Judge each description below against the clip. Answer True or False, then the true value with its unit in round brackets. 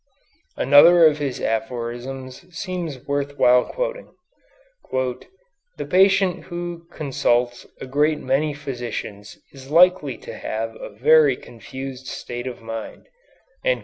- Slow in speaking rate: True (115 wpm)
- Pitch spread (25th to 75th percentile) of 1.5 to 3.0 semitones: False (5.3 semitones)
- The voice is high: False (140 Hz)